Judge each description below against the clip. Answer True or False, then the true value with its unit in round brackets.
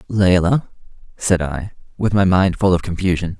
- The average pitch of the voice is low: True (90 Hz)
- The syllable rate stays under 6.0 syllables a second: True (4.8 syllables/s)